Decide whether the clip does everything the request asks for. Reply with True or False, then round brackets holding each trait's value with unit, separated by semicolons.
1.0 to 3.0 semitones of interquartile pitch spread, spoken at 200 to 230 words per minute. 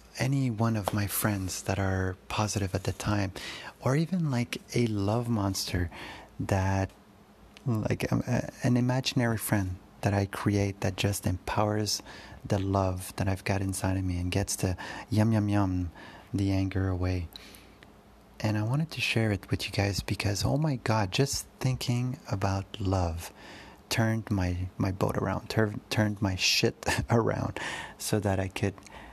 False (2.7 semitones; 160 wpm)